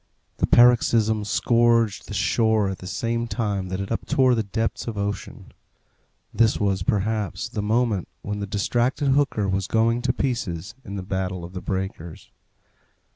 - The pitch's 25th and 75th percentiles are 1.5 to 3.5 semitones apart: Yes, average, 3.2 semitones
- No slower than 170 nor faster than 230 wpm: No, average, 160 wpm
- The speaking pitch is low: Yes, low, 105 Hz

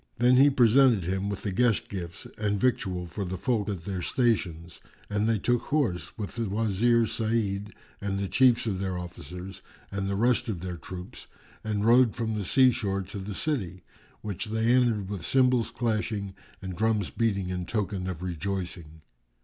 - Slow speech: No, average, 180 wpm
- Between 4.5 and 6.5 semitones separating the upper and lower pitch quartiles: No, average, 3.8 semitones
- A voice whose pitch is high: No, low, 100 Hz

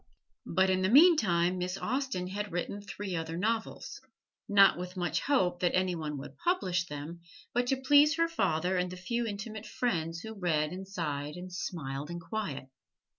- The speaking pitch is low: No, medium, 185 Hz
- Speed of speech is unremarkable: Yes, average, 175 wpm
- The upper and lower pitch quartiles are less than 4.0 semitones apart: No, average, 4.3 semitones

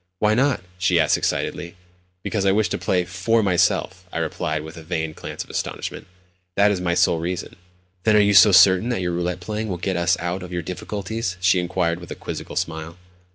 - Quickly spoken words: Yes, fast, 210 wpm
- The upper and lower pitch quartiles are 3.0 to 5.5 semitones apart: No, narrow, 2.5 semitones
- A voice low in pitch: Yes, very low, 90 Hz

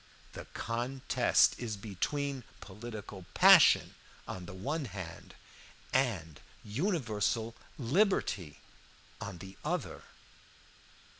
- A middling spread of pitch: No, wide, 5.7 semitones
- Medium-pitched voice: No, low, 110 Hz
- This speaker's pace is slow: Yes, slow, 85 wpm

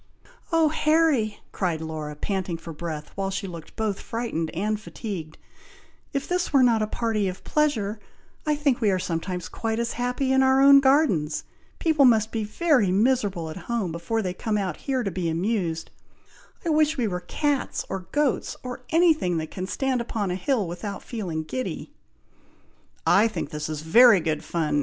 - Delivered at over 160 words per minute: Yes, average, 180 wpm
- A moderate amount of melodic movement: No, wide, 7.0 semitones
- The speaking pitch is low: No, high, 215 Hz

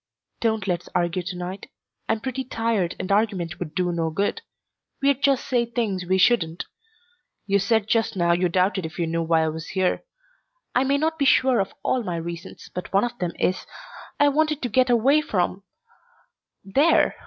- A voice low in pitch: No, high, 195 Hz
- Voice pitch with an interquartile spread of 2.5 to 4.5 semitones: No, wide, 5.5 semitones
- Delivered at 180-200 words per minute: Yes, average, 190 wpm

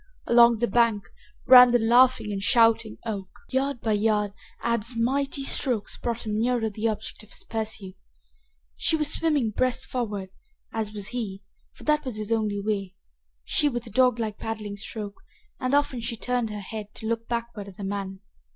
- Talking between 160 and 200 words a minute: Yes, average, 180 wpm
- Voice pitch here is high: Yes, high, 225 Hz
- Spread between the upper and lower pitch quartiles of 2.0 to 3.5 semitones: Yes, average, 2.8 semitones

